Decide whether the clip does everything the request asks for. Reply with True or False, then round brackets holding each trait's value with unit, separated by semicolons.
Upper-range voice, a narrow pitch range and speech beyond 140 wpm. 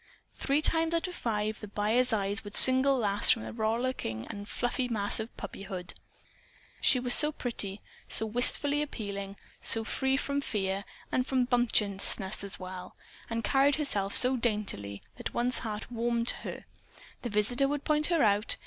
False (230 Hz; 4.3 semitones; 165 wpm)